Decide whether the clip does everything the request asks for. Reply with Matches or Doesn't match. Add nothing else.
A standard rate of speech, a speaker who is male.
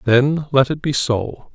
Matches